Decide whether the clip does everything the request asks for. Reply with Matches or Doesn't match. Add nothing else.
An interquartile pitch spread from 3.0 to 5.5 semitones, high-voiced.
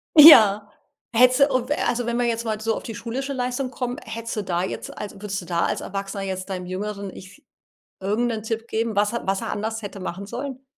Matches